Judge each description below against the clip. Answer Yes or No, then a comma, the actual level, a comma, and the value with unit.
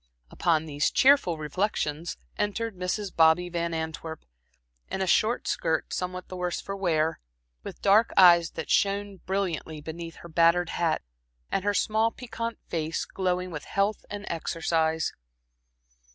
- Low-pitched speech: No, medium, 175 Hz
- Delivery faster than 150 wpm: No, average, 140 wpm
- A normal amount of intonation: Yes, average, 3.5 semitones